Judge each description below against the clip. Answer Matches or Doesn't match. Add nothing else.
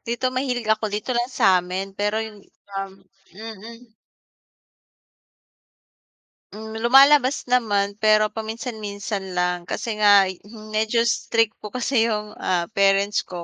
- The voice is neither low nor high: Doesn't match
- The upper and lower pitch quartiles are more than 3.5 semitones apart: Doesn't match